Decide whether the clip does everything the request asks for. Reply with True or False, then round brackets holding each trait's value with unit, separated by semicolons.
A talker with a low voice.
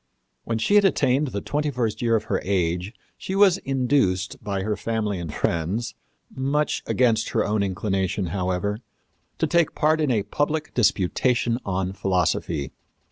True (110 Hz)